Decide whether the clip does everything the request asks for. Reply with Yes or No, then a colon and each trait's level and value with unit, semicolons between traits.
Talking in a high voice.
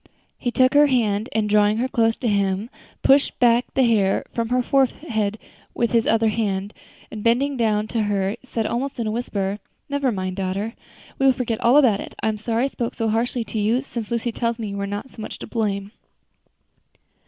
Yes: high, 225 Hz